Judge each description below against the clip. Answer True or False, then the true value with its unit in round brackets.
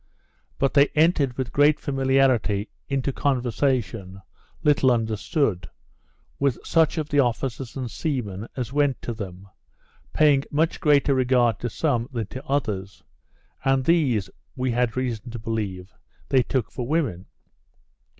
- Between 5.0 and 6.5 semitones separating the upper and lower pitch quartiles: False (3.8 semitones)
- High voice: False (130 Hz)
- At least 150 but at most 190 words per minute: False (135 wpm)